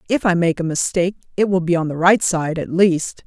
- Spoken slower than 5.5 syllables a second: No, 5.6 syllables/s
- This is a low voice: No, medium, 175 Hz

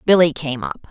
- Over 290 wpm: No, average, 200 wpm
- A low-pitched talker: No, medium, 155 Hz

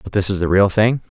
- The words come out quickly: Yes, fast, 305 wpm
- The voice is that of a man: Yes, male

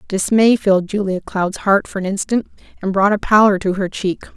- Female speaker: Yes, female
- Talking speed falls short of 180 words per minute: No, fast, 205 wpm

